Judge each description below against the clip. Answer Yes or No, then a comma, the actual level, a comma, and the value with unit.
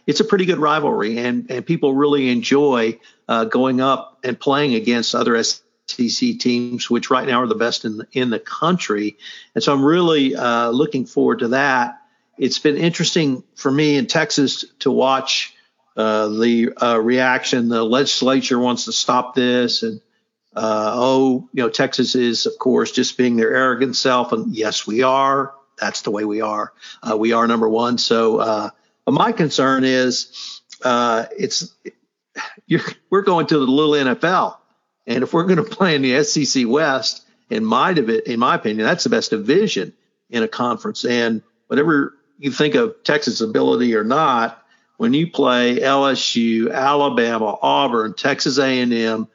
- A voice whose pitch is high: No, low, 130 Hz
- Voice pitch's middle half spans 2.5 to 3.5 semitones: No, average, 4.0 semitones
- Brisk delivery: No, average, 170 wpm